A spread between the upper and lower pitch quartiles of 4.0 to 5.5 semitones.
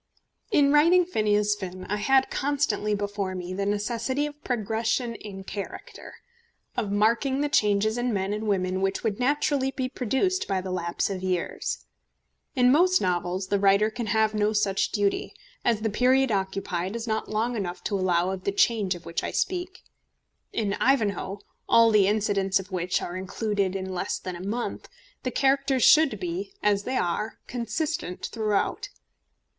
Yes: average, 4.6 semitones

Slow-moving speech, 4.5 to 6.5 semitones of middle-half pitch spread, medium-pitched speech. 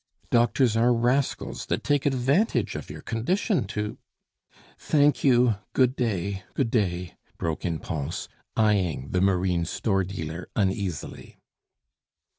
No: slow, 125 wpm; wide, 5.5 semitones; low, 105 Hz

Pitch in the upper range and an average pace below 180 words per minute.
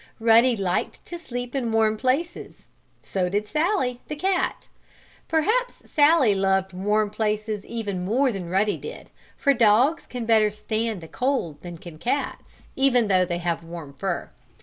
Yes: high, 220 Hz; average, 155 wpm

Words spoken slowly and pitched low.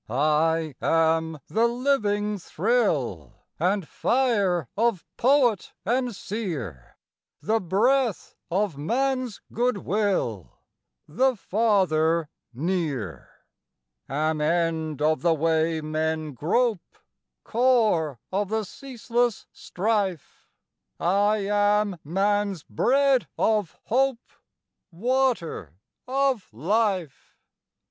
No: slow, 85 wpm; high, 195 Hz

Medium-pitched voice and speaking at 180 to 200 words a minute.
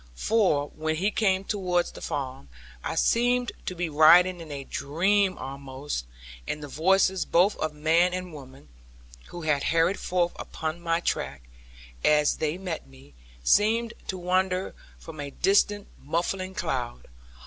No: medium, 170 Hz; average, 150 wpm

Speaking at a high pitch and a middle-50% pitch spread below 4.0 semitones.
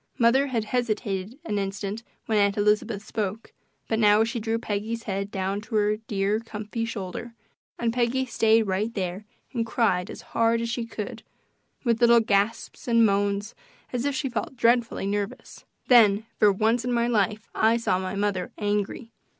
Yes: high, 220 Hz; narrow, 2.4 semitones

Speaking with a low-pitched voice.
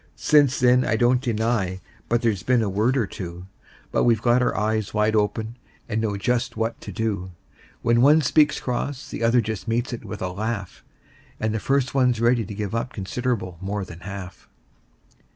Yes: low, 115 Hz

